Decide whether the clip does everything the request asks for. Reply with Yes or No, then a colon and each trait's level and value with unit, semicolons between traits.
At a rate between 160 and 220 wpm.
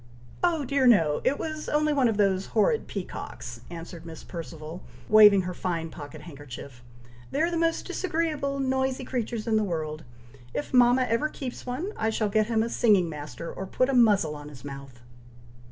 Yes: average, 185 wpm